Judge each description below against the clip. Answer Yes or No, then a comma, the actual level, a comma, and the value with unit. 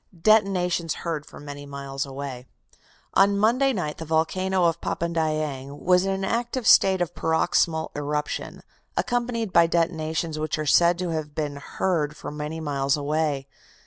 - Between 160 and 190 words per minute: No, average, 150 wpm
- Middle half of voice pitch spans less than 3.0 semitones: No, average, 3.8 semitones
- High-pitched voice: No, medium, 160 Hz